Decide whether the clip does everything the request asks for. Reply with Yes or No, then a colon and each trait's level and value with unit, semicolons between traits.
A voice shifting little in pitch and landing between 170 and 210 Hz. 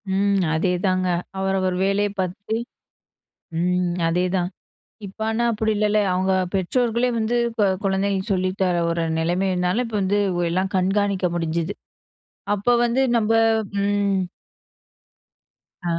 Yes: narrow, 2.2 semitones; high, 190 Hz